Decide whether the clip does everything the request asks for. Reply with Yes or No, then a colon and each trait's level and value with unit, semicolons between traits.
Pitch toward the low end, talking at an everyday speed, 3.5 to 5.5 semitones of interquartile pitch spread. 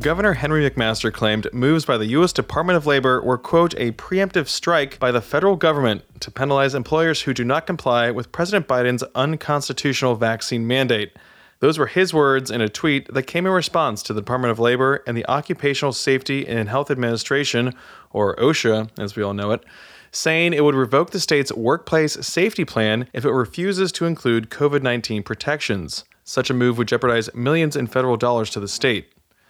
Yes: low, 130 Hz; average, 185 wpm; average, 4.5 semitones